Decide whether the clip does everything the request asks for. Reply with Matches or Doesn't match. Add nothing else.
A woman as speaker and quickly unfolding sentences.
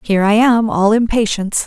Doesn't match